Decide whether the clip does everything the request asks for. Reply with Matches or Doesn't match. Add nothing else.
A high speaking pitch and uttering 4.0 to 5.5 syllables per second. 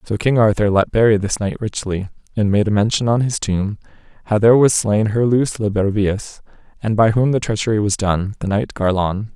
Doesn't match